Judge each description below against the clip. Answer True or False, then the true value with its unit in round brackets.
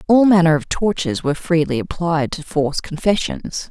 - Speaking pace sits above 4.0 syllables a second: True (5.4 syllables/s)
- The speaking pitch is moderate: True (165 Hz)